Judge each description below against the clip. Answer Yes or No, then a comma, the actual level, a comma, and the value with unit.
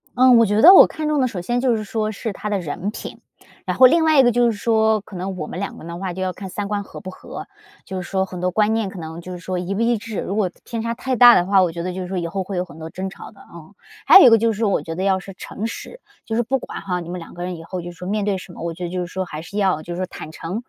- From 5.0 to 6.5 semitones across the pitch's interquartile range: No, average, 3.8 semitones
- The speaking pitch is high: Yes, high, 195 Hz